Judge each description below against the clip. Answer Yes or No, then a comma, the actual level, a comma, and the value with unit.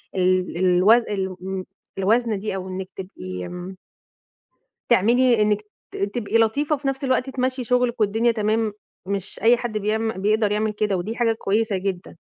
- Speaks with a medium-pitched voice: No, high, 215 Hz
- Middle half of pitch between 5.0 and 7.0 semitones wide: No, average, 3.5 semitones